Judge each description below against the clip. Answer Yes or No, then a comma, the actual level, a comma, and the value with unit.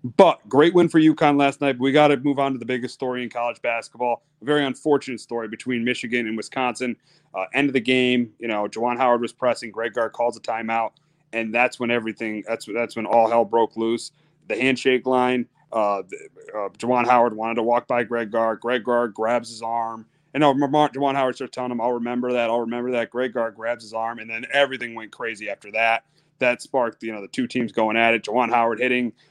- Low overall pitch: Yes, low, 120 Hz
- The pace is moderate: No, fast, 225 wpm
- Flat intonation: Yes, narrow, 2.2 semitones